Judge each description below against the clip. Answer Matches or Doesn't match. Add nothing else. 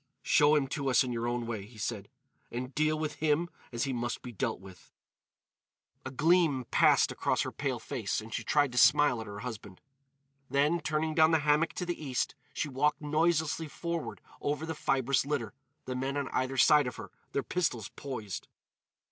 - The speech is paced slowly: Doesn't match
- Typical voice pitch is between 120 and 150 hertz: Matches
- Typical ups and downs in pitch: Matches